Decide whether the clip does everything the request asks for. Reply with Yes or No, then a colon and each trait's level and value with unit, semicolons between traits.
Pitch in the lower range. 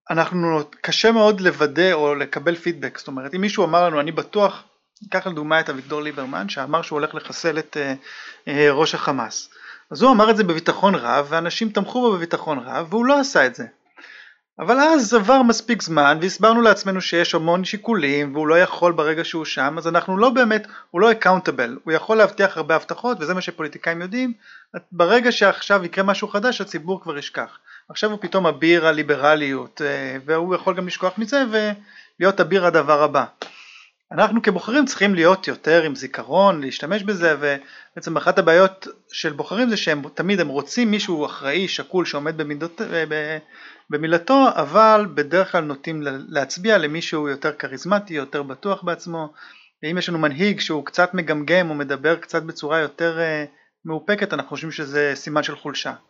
No: medium, 170 Hz